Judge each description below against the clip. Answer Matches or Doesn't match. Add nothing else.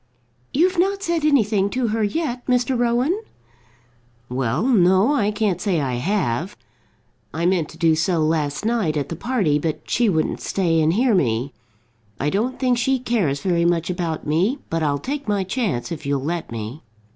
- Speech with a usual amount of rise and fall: Doesn't match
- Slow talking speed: Doesn't match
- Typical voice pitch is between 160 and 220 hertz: Matches